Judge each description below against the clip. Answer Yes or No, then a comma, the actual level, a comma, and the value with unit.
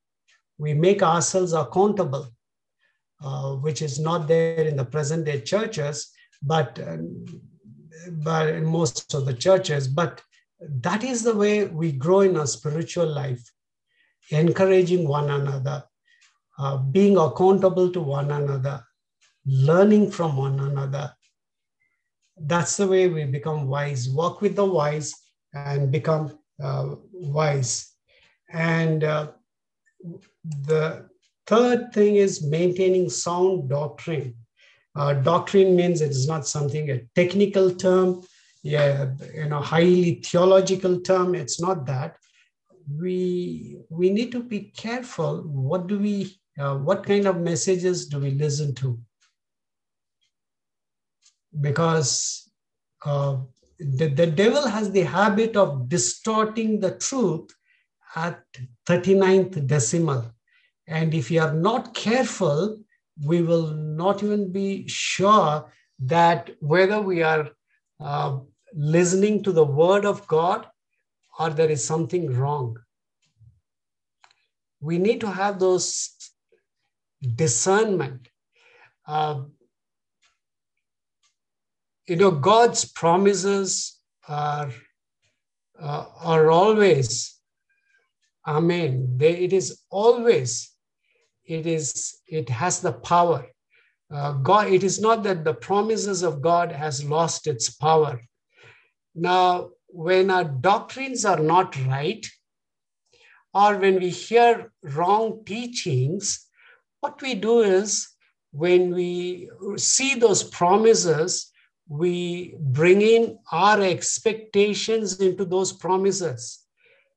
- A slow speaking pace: Yes, slow, 110 wpm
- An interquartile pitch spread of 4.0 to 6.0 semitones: Yes, average, 4.8 semitones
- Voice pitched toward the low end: No, medium, 170 Hz